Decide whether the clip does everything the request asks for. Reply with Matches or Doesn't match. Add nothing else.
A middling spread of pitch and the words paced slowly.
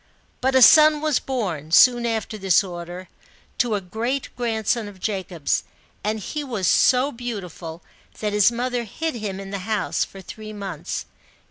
Doesn't match